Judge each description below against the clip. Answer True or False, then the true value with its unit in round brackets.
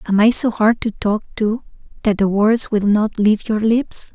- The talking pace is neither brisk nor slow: False (215 wpm)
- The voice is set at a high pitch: True (215 Hz)